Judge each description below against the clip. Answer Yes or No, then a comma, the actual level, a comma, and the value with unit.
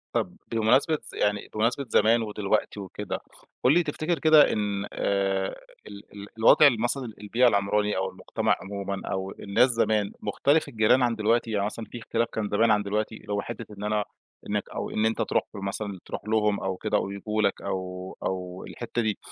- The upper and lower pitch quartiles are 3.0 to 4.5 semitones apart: No, narrow, 2.5 semitones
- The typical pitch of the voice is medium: No, low, 105 Hz